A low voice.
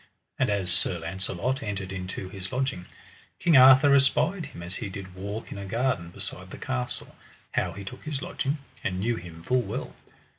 Yes: low, 100 Hz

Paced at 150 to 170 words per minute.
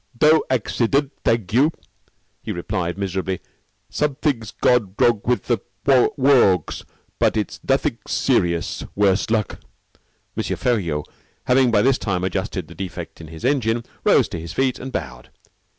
No: average, 140 wpm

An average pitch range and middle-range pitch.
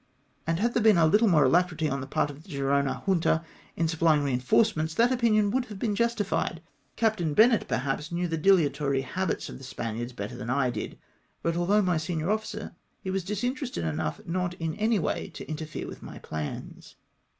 No: wide, 6.5 semitones; medium, 170 Hz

